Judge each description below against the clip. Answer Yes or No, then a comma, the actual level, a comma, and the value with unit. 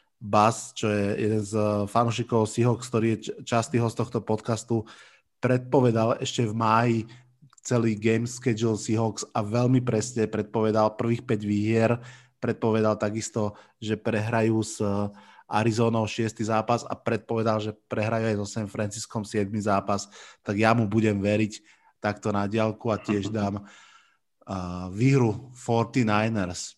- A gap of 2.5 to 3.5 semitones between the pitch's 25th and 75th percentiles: No, narrow, 1.6 semitones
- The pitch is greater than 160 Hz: No, low, 110 Hz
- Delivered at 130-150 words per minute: Yes, average, 135 wpm